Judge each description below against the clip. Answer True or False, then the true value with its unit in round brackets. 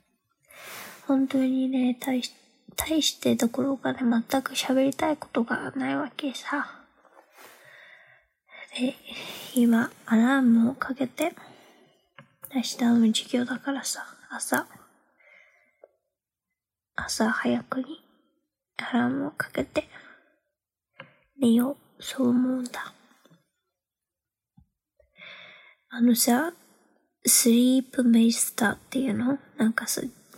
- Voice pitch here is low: False (260 Hz)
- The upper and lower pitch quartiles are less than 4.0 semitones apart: True (2.4 semitones)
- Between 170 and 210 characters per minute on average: True (180 characters per minute)